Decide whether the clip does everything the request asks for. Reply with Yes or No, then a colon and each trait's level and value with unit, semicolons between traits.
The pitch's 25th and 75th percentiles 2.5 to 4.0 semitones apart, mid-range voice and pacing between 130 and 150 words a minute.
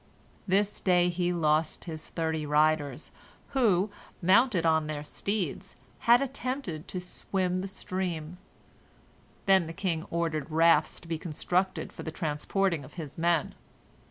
Yes: average, 3.3 semitones; medium, 170 Hz; slow, 135 wpm